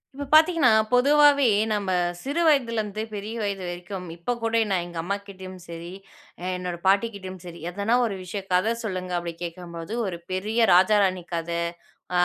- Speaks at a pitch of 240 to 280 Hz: No, high, 195 Hz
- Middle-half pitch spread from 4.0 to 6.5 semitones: Yes, average, 4.3 semitones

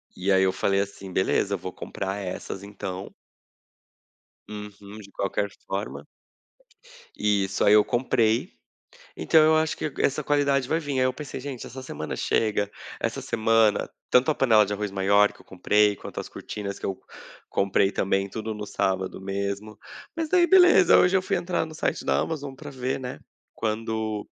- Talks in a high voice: No, low, 105 Hz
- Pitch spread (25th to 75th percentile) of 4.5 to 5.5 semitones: Yes, average, 5.2 semitones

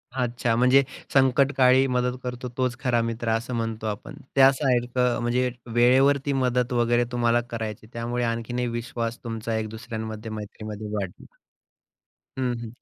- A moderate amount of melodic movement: No, narrow, 1.8 semitones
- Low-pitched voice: Yes, low, 120 Hz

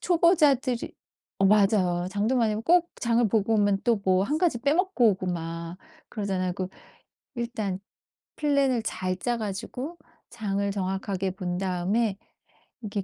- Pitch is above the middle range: Yes, high, 210 Hz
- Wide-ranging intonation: No, average, 4.4 semitones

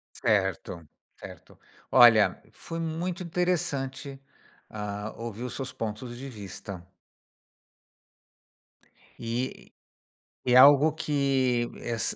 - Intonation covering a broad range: No, average, 4.3 semitones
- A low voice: Yes, low, 130 Hz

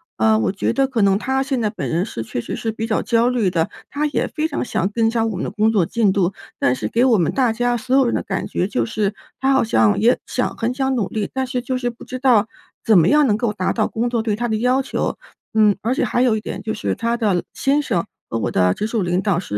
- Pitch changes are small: No, average, 4.2 semitones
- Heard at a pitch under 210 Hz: No, high, 225 Hz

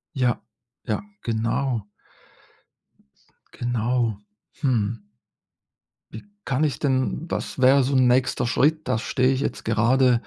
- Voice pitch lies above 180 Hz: No, low, 125 Hz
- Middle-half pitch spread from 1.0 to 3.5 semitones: Yes, narrow, 2.5 semitones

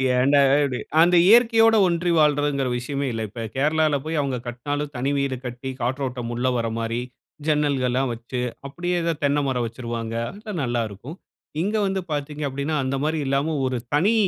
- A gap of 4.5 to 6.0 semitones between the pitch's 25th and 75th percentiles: No, average, 4.0 semitones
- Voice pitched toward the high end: No, medium, 140 Hz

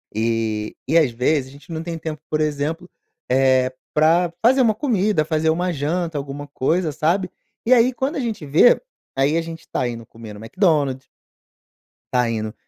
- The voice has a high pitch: No, medium, 155 Hz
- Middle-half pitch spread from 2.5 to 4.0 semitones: No, average, 5.1 semitones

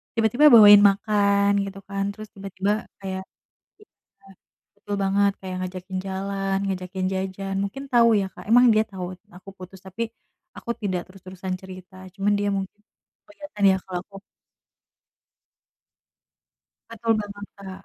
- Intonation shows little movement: Yes, narrow, 1.5 semitones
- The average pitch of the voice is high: Yes, high, 195 Hz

